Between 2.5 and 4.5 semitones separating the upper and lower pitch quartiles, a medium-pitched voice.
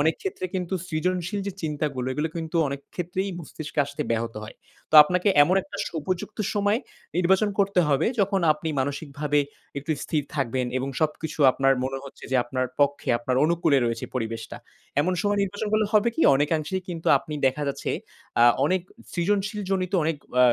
No: average, 5.0 semitones; medium, 160 Hz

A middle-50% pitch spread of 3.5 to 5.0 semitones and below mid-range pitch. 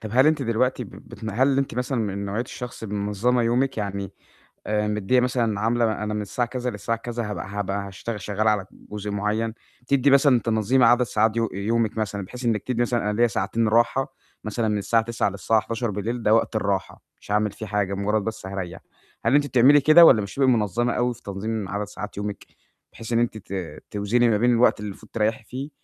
No: average, 2.9 semitones; low, 110 Hz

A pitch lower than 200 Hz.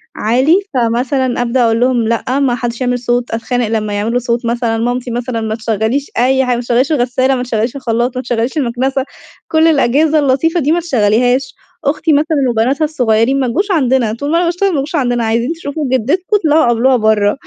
No: very high, 250 Hz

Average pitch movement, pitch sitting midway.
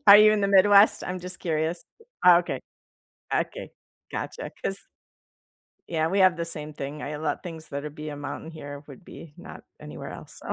Yes: average, 3.7 semitones; medium, 165 Hz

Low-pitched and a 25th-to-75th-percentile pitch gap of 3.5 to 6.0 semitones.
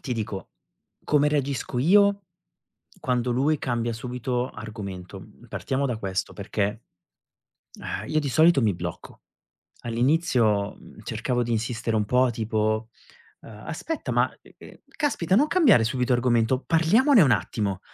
Yes: low, 125 Hz; average, 5.1 semitones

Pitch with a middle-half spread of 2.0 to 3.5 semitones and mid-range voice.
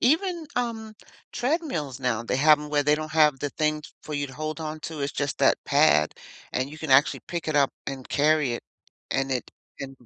Yes: narrow, 2.5 semitones; medium, 150 Hz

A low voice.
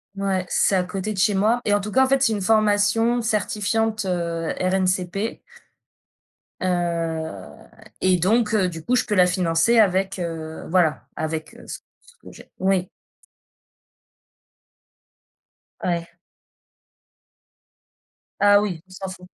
No: high, 190 Hz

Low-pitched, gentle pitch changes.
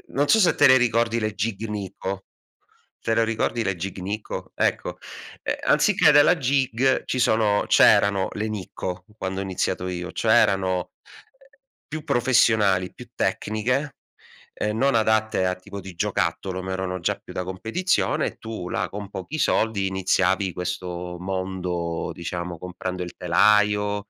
No: low, 100 Hz; average, 3.6 semitones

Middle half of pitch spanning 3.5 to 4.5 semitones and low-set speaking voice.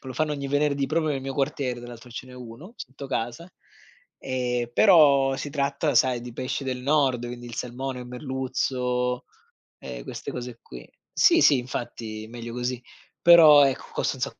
No: narrow, 2.4 semitones; low, 130 Hz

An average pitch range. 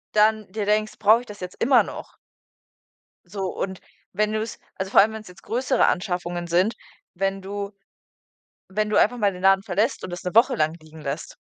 Yes: average, 3.1 semitones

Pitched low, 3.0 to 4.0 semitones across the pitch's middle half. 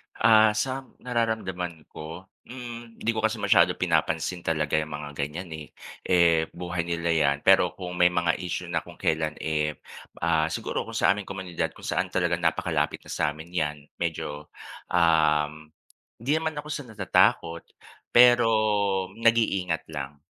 No: very low, 85 Hz; wide, 5.5 semitones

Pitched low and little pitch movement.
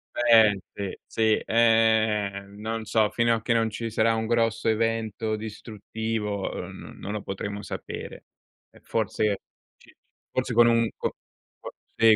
Yes: low, 110 Hz; narrow, 1.3 semitones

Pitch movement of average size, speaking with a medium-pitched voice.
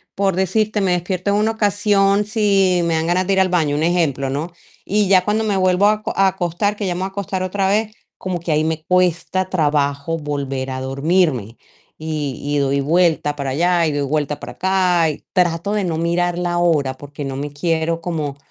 Yes: average, 4.4 semitones; medium, 175 Hz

